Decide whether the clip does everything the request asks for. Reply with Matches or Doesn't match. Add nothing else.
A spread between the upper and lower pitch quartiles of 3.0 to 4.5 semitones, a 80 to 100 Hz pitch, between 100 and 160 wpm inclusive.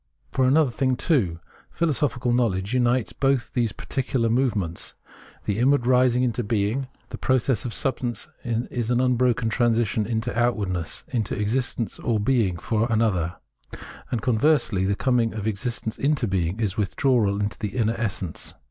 Doesn't match